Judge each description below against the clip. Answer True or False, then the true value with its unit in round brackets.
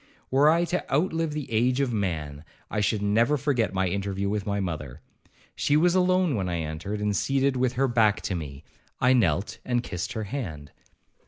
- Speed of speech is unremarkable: True (190 wpm)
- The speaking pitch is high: False (110 Hz)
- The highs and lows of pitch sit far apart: True (6.4 semitones)